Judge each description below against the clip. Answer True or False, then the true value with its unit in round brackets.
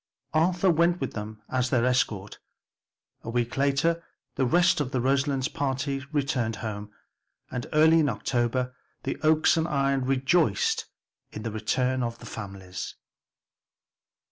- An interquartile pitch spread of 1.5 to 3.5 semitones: False (4.4 semitones)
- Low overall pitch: True (130 Hz)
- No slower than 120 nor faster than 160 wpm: True (140 wpm)